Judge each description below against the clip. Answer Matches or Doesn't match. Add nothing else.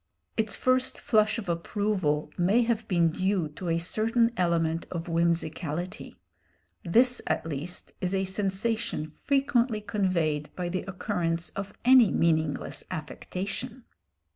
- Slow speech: Matches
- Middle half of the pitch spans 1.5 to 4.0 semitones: Doesn't match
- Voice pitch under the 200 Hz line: Matches